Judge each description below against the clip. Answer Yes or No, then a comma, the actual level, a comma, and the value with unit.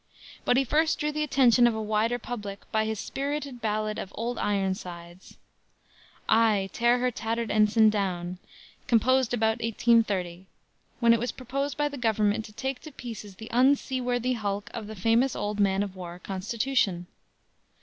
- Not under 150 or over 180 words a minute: Yes, average, 160 wpm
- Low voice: No, high, 225 Hz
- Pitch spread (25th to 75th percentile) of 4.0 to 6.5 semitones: No, average, 3.3 semitones